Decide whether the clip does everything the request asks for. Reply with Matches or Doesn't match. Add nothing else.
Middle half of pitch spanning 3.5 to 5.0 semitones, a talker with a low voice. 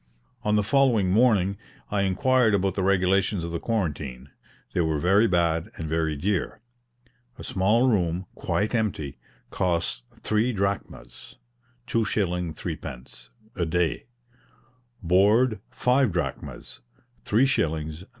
Matches